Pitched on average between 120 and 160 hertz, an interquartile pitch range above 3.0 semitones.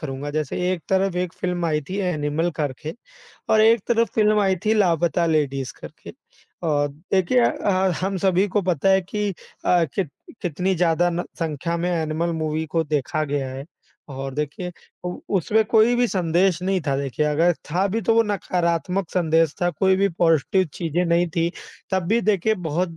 No: medium, 175 Hz; average, 3.7 semitones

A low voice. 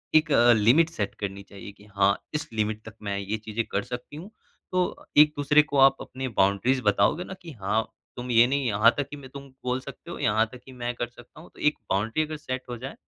Yes: low, 120 Hz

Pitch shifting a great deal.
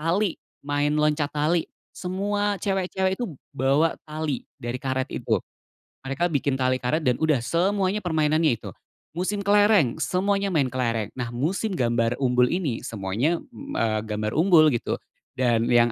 Yes: wide, 6.8 semitones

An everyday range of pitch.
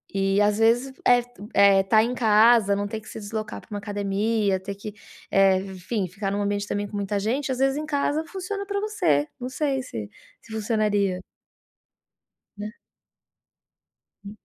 Yes: average, 3.5 semitones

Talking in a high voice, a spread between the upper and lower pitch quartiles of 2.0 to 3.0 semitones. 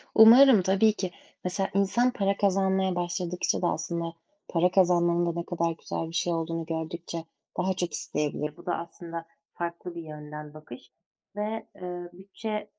No: medium, 175 Hz; narrow, 2.5 semitones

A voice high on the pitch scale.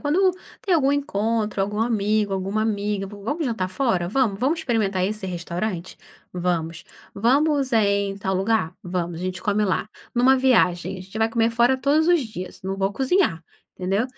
Yes: high, 210 Hz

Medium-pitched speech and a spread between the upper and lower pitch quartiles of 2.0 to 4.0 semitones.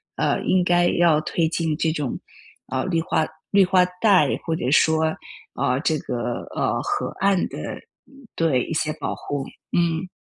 Yes: medium, 165 Hz; average, 2.9 semitones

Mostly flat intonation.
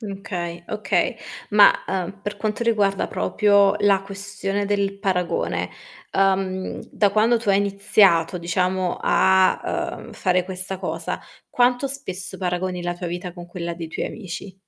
Yes: narrow, 2.0 semitones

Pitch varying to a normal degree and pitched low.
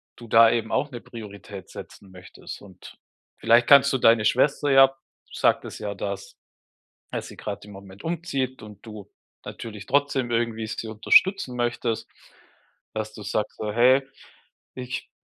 Yes: average, 3.7 semitones; low, 115 Hz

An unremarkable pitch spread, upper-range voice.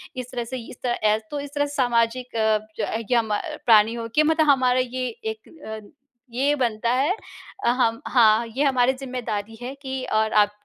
Yes: average, 3.0 semitones; high, 245 Hz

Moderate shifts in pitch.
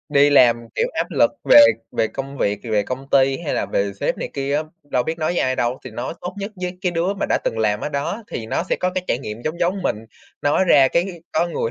No: wide, 6.4 semitones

